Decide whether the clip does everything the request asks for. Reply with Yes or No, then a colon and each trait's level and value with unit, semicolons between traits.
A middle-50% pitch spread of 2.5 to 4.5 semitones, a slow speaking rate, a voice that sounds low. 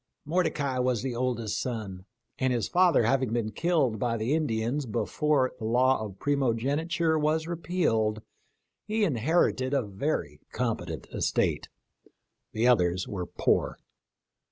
No: wide, 5.5 semitones; slow, 130 wpm; low, 130 Hz